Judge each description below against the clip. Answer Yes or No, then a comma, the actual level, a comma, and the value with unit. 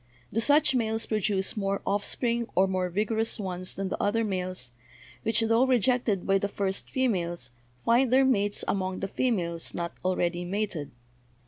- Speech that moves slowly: No, average, 155 wpm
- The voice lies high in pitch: Yes, high, 200 Hz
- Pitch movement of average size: Yes, average, 3.7 semitones